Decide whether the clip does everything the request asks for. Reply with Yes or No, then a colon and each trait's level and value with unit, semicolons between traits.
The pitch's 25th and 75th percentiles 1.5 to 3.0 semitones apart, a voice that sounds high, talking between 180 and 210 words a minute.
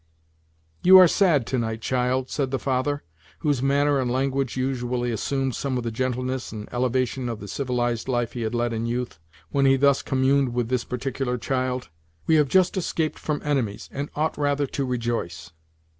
No: narrow, 2.4 semitones; low, 130 Hz; average, 185 wpm